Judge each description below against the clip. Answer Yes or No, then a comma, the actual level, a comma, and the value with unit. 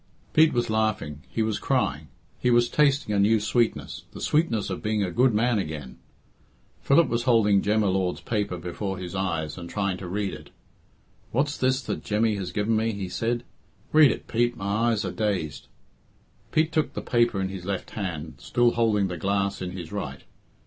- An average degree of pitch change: Yes, average, 4.0 semitones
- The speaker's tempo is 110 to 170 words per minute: No, average, 190 wpm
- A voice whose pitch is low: Yes, low, 105 Hz